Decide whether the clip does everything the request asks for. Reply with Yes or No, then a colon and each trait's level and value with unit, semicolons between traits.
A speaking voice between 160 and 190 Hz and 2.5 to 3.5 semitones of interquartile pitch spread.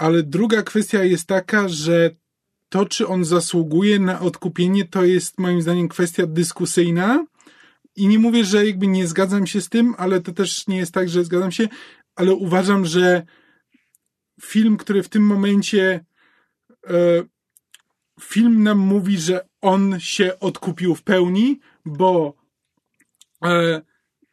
Yes: medium, 185 Hz; average, 2.8 semitones